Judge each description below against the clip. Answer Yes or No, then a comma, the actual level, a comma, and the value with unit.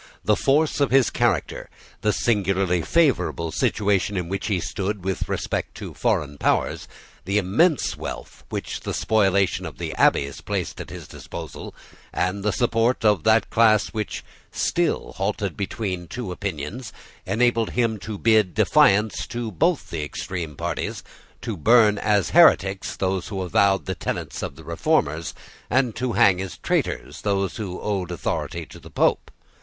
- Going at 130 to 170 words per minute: Yes, average, 160 wpm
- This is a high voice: No, low, 100 Hz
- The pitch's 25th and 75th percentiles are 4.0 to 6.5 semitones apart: No, average, 3.6 semitones